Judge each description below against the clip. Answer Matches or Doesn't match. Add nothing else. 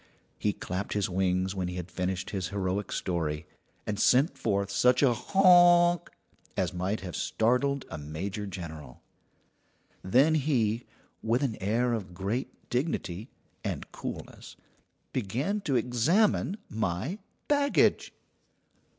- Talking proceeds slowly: Matches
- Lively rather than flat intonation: Matches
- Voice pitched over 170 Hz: Doesn't match